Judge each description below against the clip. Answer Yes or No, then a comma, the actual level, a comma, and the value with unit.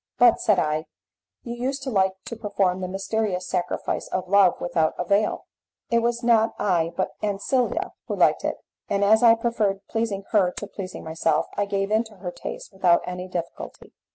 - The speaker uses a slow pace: No, average, 185 wpm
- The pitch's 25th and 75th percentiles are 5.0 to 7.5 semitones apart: No, average, 3.5 semitones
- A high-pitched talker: Yes, high, 200 Hz